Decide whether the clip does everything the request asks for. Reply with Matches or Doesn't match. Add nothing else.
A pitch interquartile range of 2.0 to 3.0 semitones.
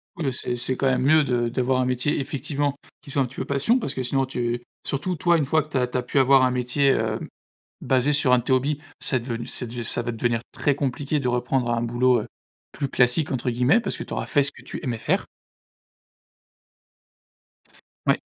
Matches